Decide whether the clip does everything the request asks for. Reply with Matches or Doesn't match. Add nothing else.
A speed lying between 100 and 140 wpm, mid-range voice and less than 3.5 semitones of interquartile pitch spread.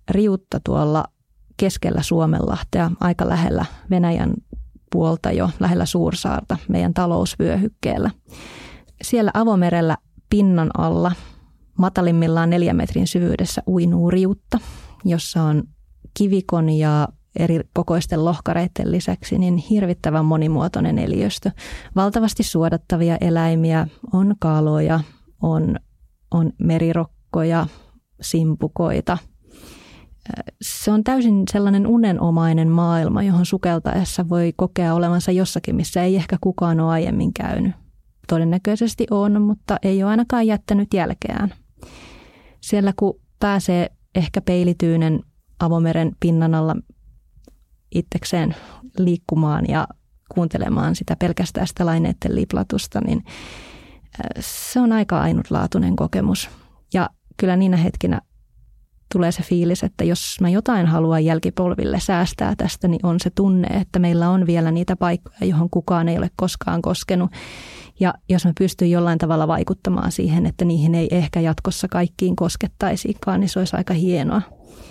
Matches